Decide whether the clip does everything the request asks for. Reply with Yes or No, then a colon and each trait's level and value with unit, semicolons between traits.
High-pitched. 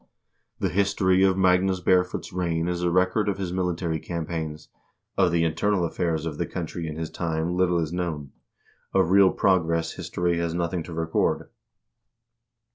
No: very low, 85 Hz